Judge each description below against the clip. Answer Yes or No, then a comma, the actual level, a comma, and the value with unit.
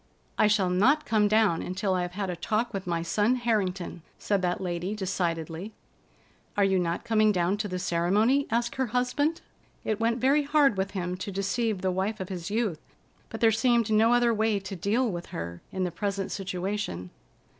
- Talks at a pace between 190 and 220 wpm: Yes, average, 195 wpm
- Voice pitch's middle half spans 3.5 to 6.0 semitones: Yes, average, 3.8 semitones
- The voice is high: Yes, high, 200 Hz